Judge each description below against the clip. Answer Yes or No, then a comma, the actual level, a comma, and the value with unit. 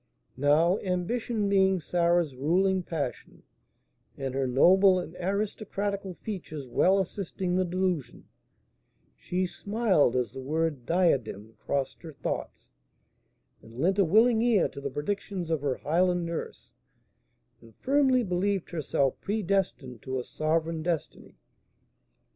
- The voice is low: No, medium, 175 Hz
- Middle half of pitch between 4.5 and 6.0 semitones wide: Yes, average, 5.1 semitones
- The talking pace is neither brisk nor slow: No, slow, 125 wpm